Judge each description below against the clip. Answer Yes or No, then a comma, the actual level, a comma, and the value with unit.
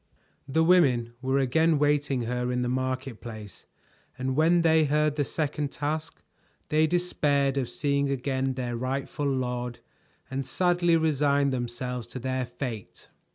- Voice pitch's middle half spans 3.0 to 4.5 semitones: Yes, average, 3.3 semitones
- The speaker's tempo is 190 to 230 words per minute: No, average, 145 wpm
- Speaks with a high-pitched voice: No, low, 135 Hz